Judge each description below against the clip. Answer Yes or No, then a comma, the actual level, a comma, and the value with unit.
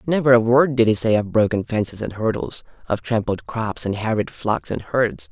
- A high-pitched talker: No, low, 110 Hz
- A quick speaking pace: Yes, fast, 215 wpm